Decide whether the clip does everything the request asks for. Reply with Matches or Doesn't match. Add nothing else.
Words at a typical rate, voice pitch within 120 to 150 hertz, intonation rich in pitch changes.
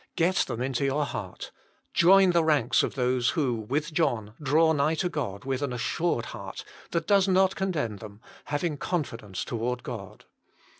Matches